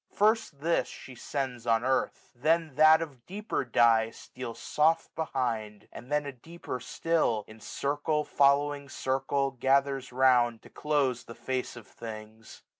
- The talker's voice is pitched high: No, low, 135 Hz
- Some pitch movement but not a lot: Yes, average, 3.8 semitones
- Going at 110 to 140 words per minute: No, average, 155 wpm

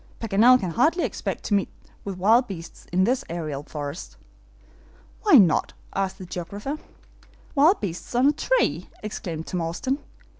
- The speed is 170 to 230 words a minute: No, average, 150 wpm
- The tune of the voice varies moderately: No, wide, 6.8 semitones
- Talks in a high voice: Yes, high, 195 Hz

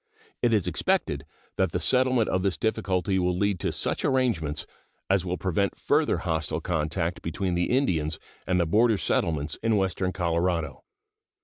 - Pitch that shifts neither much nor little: Yes, average, 3.6 semitones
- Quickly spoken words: No, average, 155 wpm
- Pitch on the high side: No, very low, 90 Hz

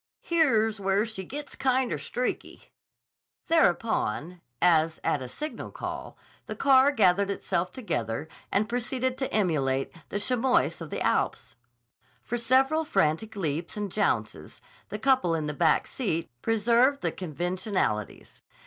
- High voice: Yes, high, 205 Hz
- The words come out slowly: Yes, slow, 130 wpm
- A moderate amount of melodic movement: No, wide, 7.2 semitones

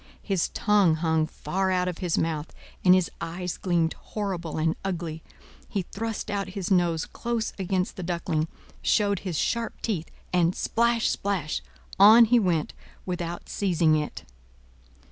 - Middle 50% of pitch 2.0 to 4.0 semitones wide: Yes, average, 3.4 semitones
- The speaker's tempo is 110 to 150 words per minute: Yes, average, 140 wpm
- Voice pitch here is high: No, medium, 180 Hz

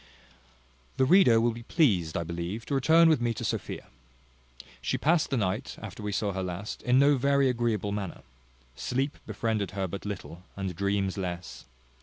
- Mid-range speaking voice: No, low, 105 Hz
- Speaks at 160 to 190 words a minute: Yes, average, 175 wpm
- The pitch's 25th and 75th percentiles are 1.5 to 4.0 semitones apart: No, wide, 5.5 semitones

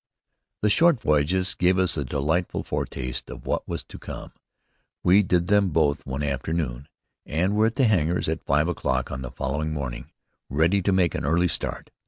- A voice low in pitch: Yes, very low, 80 Hz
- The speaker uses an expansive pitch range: No, average, 4.8 semitones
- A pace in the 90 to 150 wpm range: No, average, 185 wpm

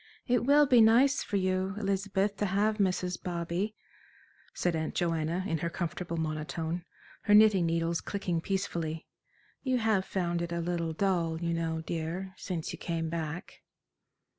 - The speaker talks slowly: No, average, 155 wpm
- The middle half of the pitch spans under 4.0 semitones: Yes, average, 3.2 semitones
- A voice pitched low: No, medium, 175 Hz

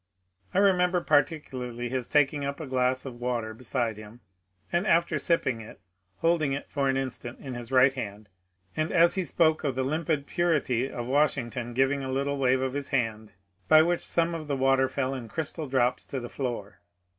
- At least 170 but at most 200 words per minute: Yes, average, 190 wpm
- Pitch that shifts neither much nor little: Yes, average, 3.8 semitones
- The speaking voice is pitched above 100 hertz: Yes, low, 135 Hz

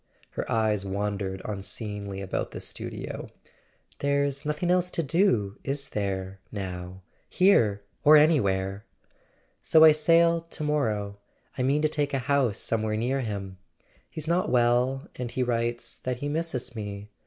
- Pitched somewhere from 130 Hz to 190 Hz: No, low, 120 Hz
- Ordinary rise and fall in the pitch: No, wide, 6.5 semitones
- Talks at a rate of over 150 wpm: No, average, 145 wpm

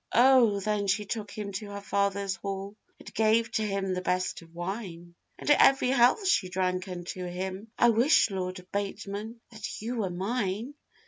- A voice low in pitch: No, high, 200 Hz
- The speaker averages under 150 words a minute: No, average, 175 wpm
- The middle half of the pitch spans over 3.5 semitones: No, average, 3.2 semitones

